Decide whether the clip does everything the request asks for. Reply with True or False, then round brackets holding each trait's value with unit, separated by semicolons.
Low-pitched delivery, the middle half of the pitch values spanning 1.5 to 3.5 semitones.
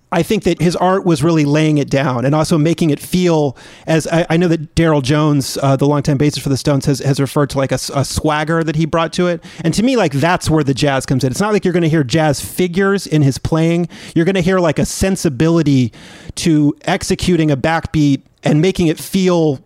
False (160 Hz; 3.1 semitones)